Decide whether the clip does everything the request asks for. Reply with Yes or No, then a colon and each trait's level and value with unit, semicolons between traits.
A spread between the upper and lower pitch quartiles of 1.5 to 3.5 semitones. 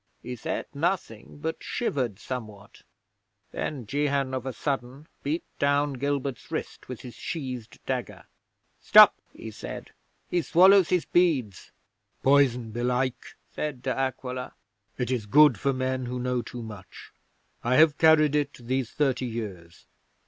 Yes: average, 3.2 semitones